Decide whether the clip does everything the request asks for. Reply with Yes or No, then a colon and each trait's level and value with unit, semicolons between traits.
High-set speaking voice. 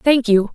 Yes: high, 235 Hz